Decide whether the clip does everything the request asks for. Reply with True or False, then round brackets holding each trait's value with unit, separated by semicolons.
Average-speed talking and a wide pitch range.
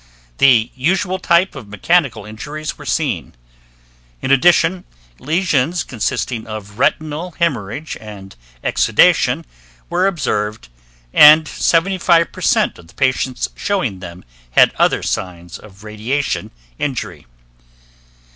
False (105 wpm; 7.9 semitones)